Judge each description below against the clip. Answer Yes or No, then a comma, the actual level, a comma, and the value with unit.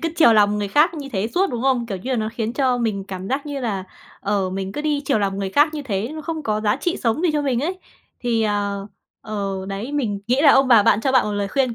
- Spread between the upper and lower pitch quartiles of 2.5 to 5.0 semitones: No, wide, 5.5 semitones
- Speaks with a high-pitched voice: Yes, high, 230 Hz